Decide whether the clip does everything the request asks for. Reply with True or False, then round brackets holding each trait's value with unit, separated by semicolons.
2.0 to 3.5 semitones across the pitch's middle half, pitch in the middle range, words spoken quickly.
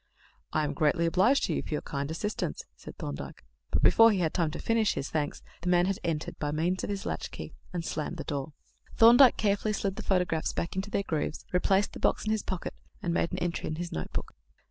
False (4.2 semitones; 175 Hz; 230 wpm)